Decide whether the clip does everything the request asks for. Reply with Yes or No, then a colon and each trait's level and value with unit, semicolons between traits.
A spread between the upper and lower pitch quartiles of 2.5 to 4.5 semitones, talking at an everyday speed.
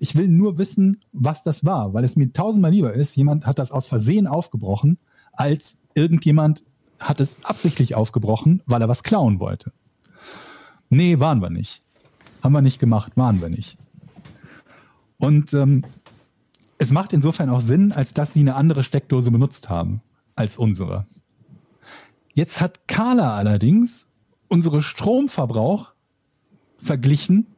No: average, 5.2 semitones; average, 140 wpm